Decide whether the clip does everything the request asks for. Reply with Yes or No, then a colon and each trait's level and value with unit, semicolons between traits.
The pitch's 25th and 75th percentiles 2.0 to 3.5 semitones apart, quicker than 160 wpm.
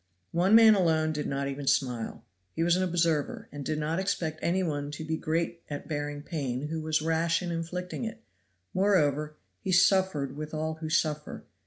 Yes: average, 2.7 semitones; average, 185 wpm